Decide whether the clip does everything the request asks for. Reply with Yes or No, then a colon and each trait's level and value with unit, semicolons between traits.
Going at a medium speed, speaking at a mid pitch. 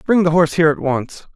No: fast, 265 wpm; medium, 160 Hz